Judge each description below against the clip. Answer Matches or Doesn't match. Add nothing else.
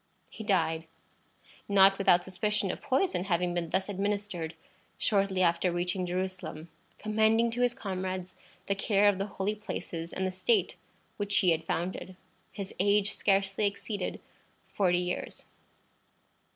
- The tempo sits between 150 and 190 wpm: Doesn't match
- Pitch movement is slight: Matches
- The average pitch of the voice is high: Matches